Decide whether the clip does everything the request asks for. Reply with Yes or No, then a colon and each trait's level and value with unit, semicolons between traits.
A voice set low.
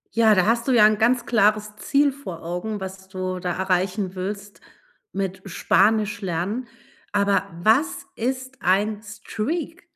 No: high, 210 Hz